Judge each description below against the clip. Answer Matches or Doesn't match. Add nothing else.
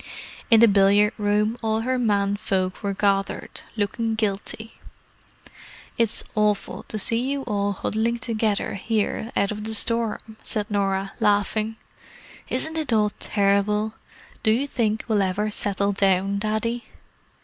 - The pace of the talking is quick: Doesn't match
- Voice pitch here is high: Matches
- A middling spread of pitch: Doesn't match